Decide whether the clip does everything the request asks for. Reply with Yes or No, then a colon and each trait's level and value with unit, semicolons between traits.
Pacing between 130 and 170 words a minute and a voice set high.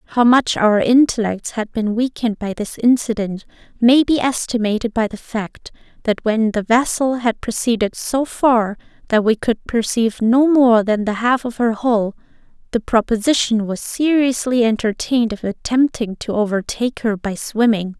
Yes: average, 160 wpm; high, 230 Hz